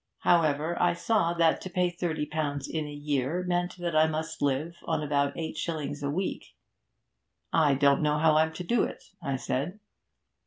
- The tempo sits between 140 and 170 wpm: No, average, 185 wpm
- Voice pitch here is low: No, medium, 155 Hz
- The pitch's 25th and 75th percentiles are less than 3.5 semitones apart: Yes, average, 2.9 semitones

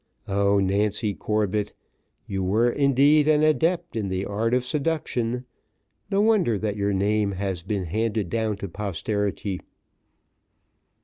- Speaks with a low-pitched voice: Yes, low, 105 Hz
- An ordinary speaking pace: No, slow, 130 wpm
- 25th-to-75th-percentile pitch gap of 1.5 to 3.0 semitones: No, average, 4.0 semitones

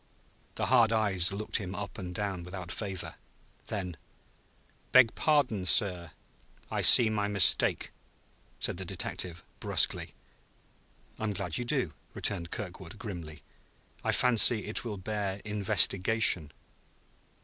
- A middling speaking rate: No, slow, 125 wpm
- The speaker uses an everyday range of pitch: Yes, average, 3.1 semitones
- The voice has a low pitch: Yes, low, 100 Hz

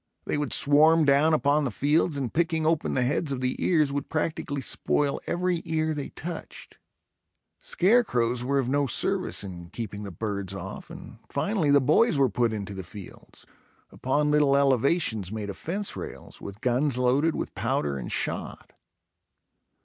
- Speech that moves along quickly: No, average, 170 wpm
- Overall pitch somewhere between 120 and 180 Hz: Yes, medium, 140 Hz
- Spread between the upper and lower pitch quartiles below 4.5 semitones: No, average, 5.2 semitones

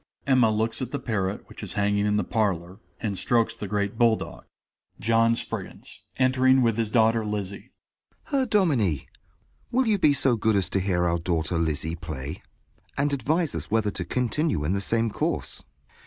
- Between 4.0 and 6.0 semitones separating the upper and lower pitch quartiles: Yes, average, 4.8 semitones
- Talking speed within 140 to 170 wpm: No, average, 180 wpm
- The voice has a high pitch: No, low, 110 Hz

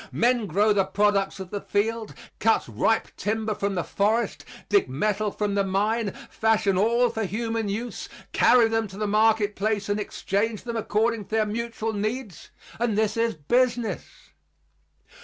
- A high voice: Yes, high, 215 Hz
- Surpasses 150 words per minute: Yes, average, 160 wpm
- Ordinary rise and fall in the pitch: No, narrow, 2.0 semitones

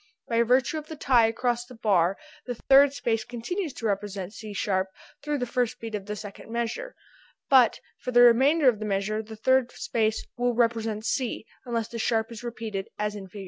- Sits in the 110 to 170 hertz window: No, high, 230 Hz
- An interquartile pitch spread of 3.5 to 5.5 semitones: No, average, 2.7 semitones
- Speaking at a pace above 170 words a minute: Yes, average, 200 wpm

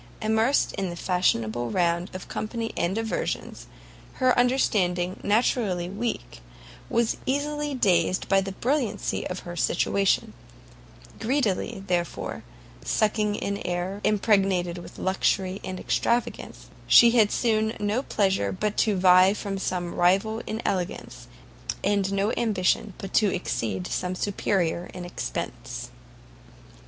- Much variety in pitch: No, average, 3.5 semitones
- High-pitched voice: Yes, high, 195 Hz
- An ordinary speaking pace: No, slow, 125 wpm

